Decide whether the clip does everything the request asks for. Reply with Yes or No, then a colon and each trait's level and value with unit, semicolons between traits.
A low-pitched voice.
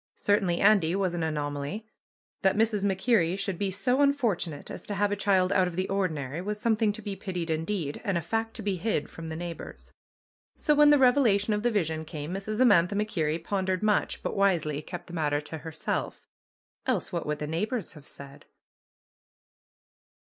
No: high, 190 Hz